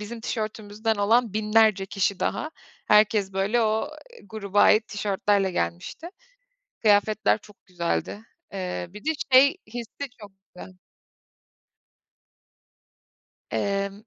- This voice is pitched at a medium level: No, high, 210 Hz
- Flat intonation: Yes, narrow, 1.9 semitones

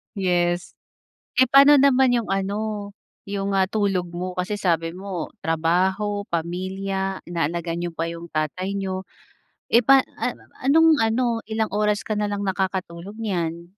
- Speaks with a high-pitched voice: Yes, high, 195 Hz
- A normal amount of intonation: Yes, average, 3.2 semitones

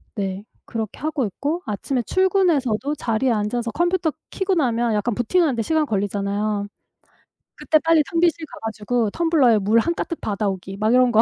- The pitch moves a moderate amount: No, wide, 7.0 semitones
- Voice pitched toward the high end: Yes, high, 240 Hz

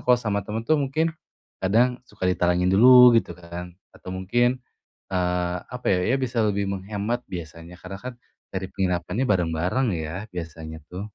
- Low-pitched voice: Yes, very low, 95 Hz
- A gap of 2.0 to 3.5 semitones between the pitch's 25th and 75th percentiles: No, average, 4.5 semitones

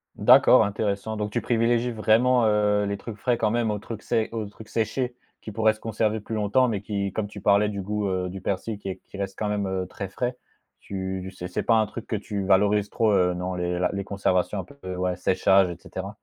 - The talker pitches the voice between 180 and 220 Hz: No, low, 105 Hz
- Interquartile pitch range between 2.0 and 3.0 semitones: Yes, narrow, 2.4 semitones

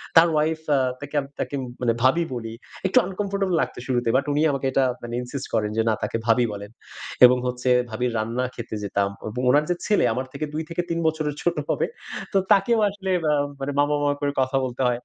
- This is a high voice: No, low, 135 Hz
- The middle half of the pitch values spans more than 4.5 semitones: Yes, average, 4.9 semitones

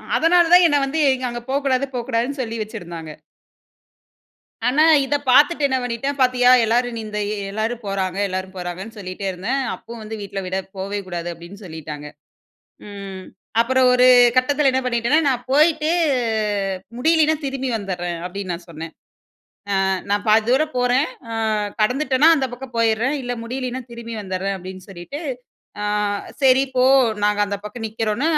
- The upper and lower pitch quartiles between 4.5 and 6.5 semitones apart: Yes, average, 5.1 semitones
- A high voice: Yes, high, 235 Hz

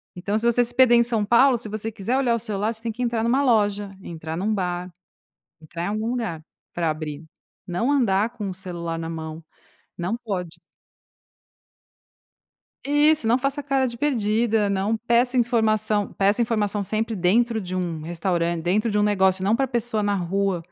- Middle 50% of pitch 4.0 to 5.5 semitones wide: Yes, average, 4.5 semitones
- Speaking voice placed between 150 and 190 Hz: No, high, 210 Hz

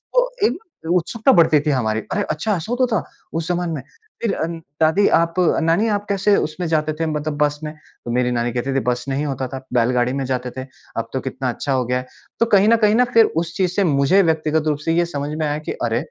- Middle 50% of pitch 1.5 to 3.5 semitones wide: No, average, 5.2 semitones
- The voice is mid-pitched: Yes, medium, 155 Hz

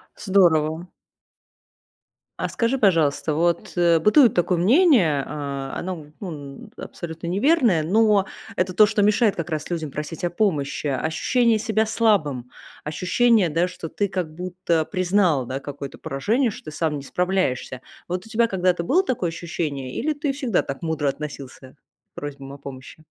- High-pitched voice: No, medium, 175 Hz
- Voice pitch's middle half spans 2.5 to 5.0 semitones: No, wide, 5.6 semitones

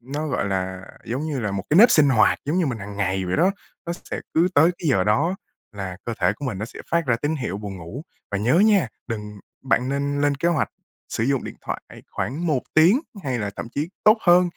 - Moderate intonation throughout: No, wide, 7.2 semitones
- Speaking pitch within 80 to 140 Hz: Yes, low, 135 Hz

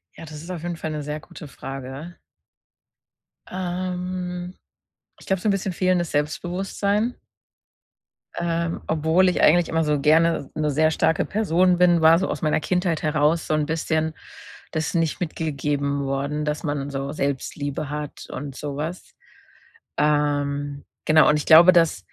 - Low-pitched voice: No, medium, 160 Hz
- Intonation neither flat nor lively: Yes, average, 3.0 semitones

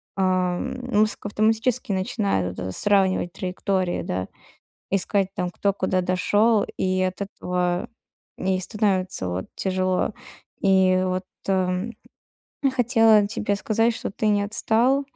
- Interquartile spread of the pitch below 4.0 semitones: Yes, narrow, 2.4 semitones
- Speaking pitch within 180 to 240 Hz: Yes, high, 190 Hz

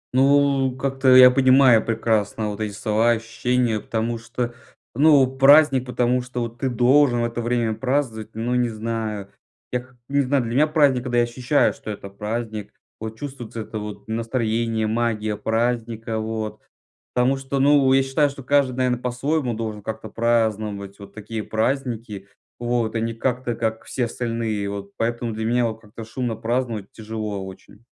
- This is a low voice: Yes, low, 115 Hz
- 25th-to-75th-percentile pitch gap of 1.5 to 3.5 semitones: Yes, narrow, 2.6 semitones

